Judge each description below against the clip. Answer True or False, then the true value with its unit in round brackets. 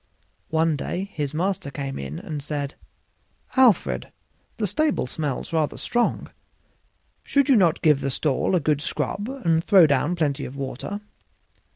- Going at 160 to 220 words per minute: False (150 wpm)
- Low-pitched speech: False (160 Hz)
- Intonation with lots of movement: True (5.7 semitones)